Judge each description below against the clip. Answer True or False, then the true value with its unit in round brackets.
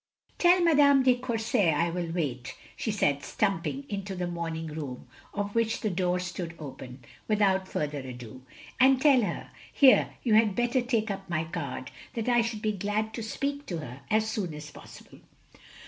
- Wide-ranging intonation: True (6.2 semitones)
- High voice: True (195 Hz)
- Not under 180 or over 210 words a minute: True (185 wpm)